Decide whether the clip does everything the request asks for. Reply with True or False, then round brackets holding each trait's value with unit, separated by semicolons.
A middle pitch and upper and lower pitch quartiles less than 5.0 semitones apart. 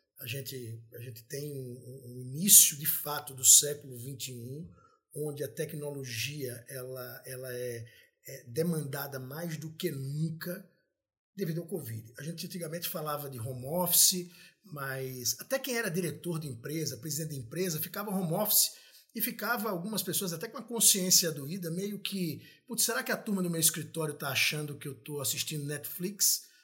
False (155 Hz; 5.3 semitones)